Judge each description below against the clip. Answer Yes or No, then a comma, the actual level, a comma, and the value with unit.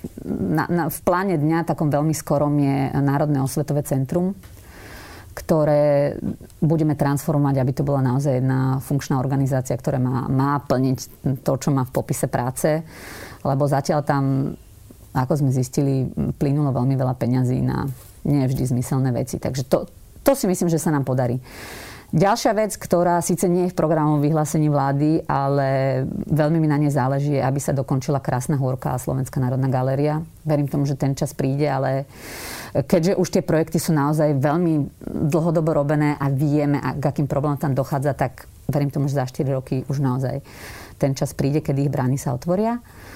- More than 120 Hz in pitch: Yes, medium, 140 Hz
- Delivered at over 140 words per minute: Yes, fast, 165 wpm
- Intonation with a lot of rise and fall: No, average, 2.7 semitones